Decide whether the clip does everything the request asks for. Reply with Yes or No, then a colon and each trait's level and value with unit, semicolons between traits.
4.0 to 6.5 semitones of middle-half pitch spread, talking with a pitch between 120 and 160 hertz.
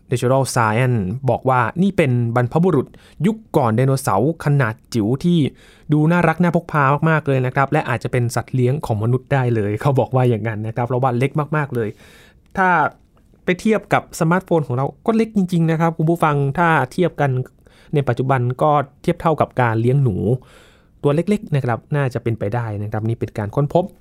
Yes: average, 4.8 semitones; low, 135 Hz